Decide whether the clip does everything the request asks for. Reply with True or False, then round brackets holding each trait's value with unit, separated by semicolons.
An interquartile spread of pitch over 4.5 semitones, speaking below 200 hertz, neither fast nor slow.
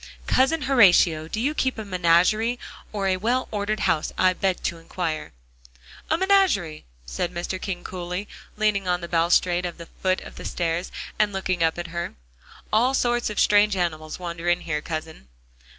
False (3.9 semitones; 185 Hz; 175 wpm)